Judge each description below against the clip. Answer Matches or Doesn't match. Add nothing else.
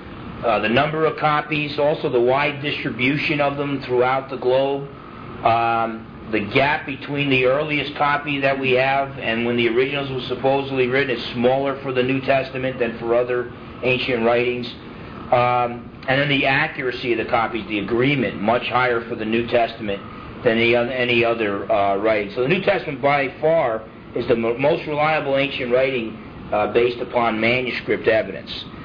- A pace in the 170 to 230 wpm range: Matches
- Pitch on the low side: Matches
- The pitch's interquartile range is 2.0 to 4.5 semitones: Matches